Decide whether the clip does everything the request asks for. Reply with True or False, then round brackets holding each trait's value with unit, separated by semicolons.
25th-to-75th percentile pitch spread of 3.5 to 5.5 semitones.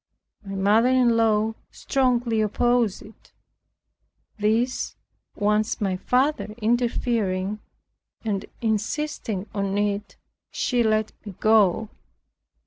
False (2.7 semitones)